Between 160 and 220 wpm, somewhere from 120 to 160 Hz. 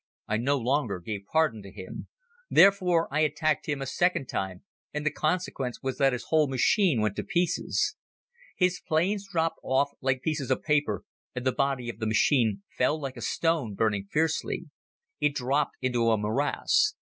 Yes: average, 175 wpm; medium, 140 Hz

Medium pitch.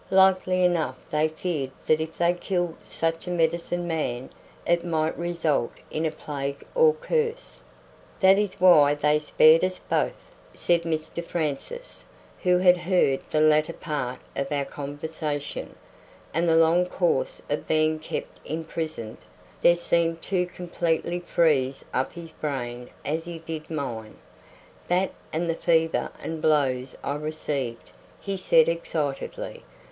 Yes: medium, 165 Hz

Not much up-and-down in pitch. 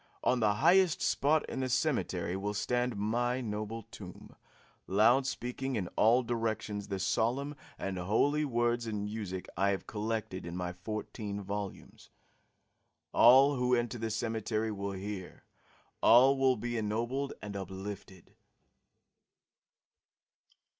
No: average, 3.6 semitones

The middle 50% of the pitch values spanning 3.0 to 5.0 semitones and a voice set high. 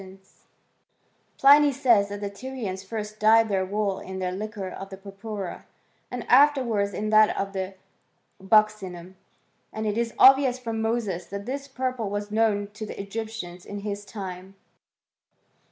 No: narrow, 2.5 semitones; high, 210 Hz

